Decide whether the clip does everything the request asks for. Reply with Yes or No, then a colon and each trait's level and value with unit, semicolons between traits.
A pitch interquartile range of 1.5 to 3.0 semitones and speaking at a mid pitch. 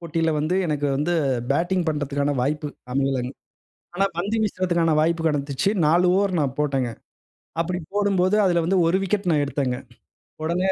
No: average, 4.0 semitones; medium, 165 Hz